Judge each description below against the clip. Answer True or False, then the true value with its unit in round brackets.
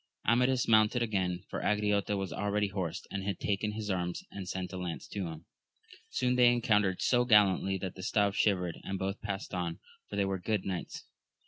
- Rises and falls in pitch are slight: True (2.3 semitones)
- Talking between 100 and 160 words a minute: False (195 wpm)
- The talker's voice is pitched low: True (100 Hz)